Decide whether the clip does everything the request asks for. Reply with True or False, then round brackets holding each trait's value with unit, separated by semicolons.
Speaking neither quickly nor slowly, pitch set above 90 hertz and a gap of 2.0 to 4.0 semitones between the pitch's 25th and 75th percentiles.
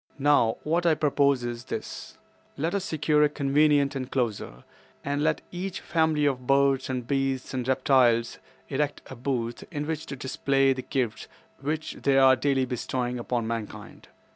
True (160 wpm; 135 Hz; 2.7 semitones)